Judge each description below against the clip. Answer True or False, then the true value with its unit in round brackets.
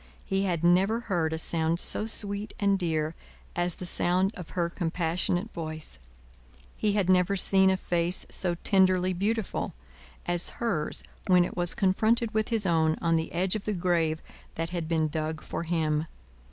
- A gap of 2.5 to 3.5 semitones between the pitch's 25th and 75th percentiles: True (2.9 semitones)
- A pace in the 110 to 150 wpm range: False (170 wpm)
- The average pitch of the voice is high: False (175 Hz)